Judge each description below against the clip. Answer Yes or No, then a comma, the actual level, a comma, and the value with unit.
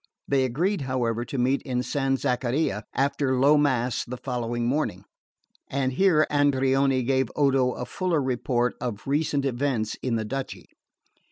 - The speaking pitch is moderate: No, low, 130 Hz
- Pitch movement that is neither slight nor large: No, narrow, 2.3 semitones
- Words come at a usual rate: Yes, average, 150 wpm